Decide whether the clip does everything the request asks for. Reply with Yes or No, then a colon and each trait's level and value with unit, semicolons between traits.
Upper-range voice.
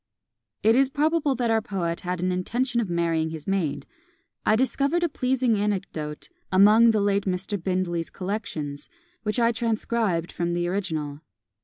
Yes: high, 200 Hz